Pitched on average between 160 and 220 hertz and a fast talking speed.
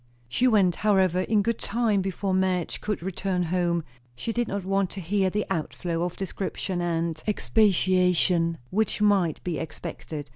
No: medium, 185 Hz; average, 155 wpm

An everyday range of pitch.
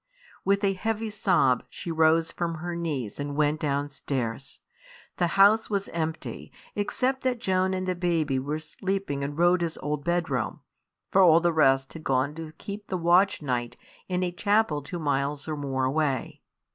Yes: average, 4.6 semitones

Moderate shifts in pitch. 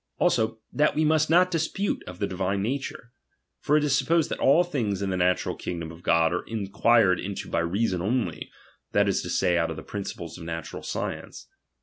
No: wide, 8.2 semitones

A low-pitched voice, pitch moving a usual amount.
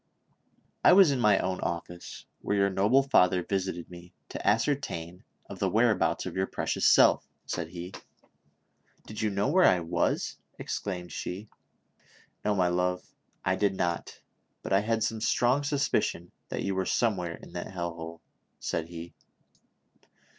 Yes: very low, 95 Hz; average, 3.5 semitones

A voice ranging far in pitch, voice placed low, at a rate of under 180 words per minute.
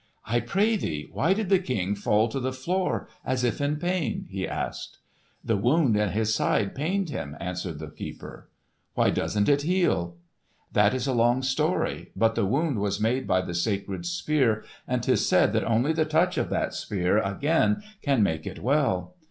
No: wide, 7.4 semitones; low, 120 Hz; average, 185 wpm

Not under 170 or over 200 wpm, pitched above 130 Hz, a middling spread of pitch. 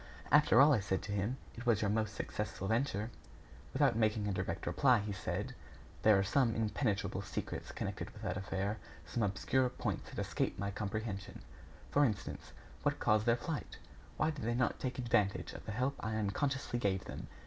No: average, 185 wpm; low, 110 Hz; average, 3.5 semitones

